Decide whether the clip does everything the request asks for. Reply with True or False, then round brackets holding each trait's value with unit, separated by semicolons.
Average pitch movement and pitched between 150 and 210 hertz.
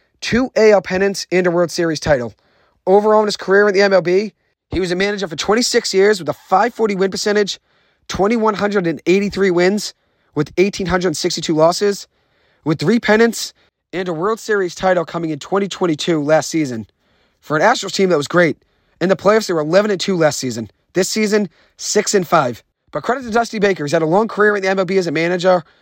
True (3.4 semitones; 190 Hz)